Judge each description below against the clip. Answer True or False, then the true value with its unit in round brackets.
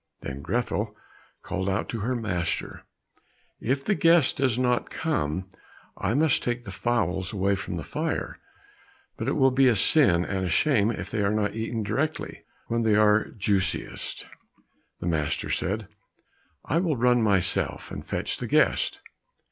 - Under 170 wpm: True (160 wpm)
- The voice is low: True (110 Hz)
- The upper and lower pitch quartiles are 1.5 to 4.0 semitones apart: False (4.4 semitones)